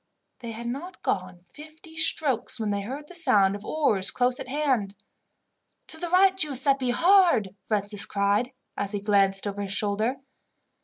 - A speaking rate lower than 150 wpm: No, average, 160 wpm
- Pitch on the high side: Yes, high, 235 Hz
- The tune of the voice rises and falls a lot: Yes, wide, 6.9 semitones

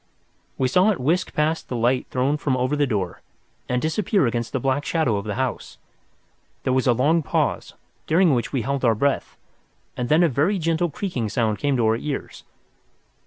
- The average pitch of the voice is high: No, low, 135 Hz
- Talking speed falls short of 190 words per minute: No, average, 195 wpm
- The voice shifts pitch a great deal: No, average, 4.6 semitones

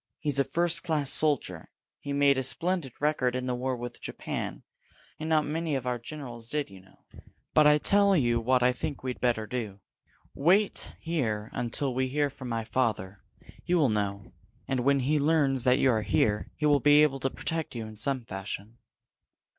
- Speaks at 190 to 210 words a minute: Yes, average, 195 wpm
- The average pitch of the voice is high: No, low, 130 Hz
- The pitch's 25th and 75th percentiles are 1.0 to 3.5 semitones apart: No, average, 4.2 semitones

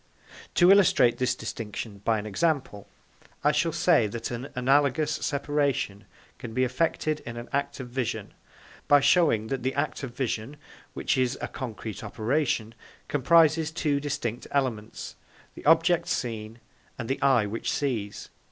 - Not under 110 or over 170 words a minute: Yes, average, 150 wpm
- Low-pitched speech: Yes, low, 130 Hz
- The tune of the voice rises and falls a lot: No, average, 4.3 semitones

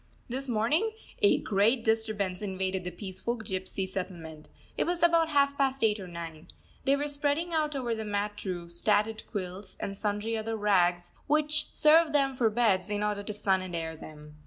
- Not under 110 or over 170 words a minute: No, average, 185 wpm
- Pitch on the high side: Yes, high, 210 Hz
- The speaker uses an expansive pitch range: Yes, wide, 6.4 semitones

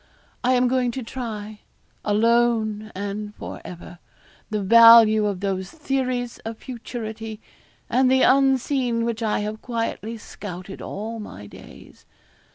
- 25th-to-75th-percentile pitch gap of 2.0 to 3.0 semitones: Yes, average, 2.7 semitones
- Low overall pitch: No, high, 225 Hz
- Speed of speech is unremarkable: No, slow, 130 wpm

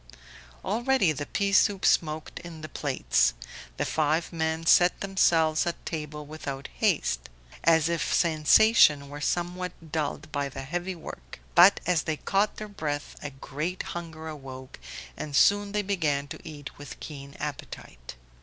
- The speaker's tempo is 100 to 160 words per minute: Yes, average, 150 wpm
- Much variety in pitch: No, average, 3.5 semitones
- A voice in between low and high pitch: Yes, medium, 160 Hz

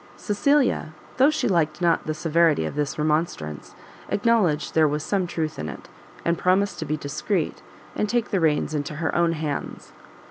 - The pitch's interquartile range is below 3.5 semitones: No, average, 3.8 semitones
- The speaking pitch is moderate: Yes, medium, 160 Hz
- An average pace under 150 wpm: No, average, 175 wpm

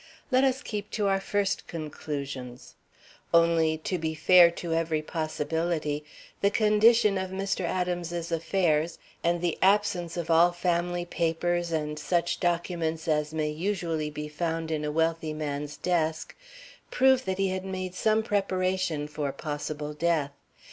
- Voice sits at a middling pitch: Yes, medium, 170 Hz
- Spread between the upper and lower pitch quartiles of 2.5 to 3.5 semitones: Yes, average, 3.1 semitones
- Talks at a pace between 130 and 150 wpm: Yes, average, 145 wpm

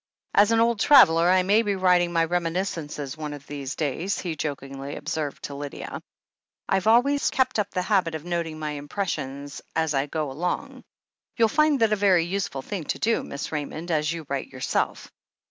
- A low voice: No, medium, 165 Hz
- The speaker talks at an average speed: Yes, average, 195 wpm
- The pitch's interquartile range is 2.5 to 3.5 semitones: No, average, 5.3 semitones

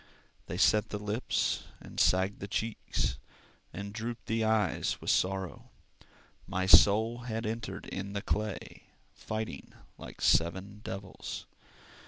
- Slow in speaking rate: Yes, slow, 125 wpm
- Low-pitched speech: Yes, low, 105 Hz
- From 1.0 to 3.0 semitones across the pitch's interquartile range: Yes, narrow, 2.5 semitones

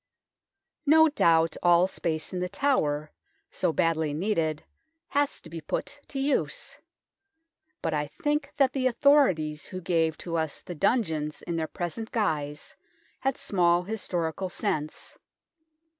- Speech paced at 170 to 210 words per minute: No, slow, 135 wpm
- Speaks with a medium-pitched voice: Yes, medium, 175 Hz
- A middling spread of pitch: No, wide, 6.8 semitones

